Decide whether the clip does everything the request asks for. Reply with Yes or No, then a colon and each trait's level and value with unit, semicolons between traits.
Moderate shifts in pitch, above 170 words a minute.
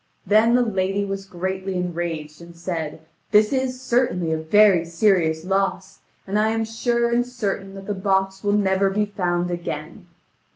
No: average, 3.3 semitones; average, 165 wpm